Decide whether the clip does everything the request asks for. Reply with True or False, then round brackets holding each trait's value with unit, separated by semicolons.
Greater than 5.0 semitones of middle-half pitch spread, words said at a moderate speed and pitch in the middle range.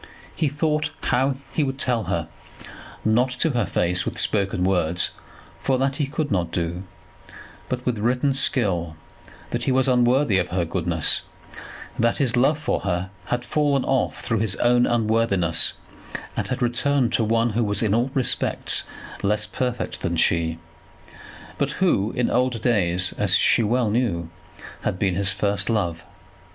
False (5.4 semitones; 160 wpm; 115 Hz)